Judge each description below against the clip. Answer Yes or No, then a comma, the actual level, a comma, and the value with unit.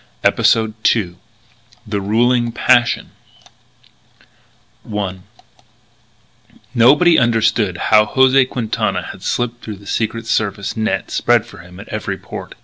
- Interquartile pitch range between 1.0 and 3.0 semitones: Yes, average, 2.7 semitones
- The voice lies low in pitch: Yes, low, 115 Hz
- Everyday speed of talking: No, slow, 115 wpm